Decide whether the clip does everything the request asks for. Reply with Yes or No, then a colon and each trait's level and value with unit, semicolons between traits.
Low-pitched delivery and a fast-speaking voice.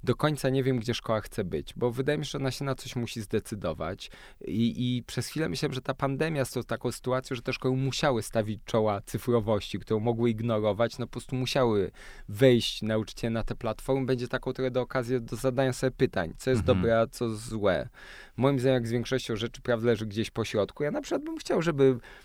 Yes: low, 125 Hz; fast, 220 wpm